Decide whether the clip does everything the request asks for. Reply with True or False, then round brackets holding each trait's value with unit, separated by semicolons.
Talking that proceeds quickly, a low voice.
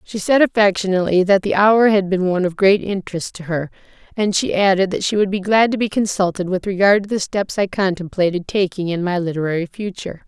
False (215 wpm; 190 Hz)